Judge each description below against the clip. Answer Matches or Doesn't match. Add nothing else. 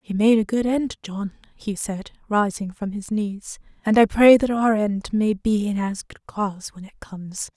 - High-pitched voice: Matches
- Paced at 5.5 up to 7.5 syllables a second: Doesn't match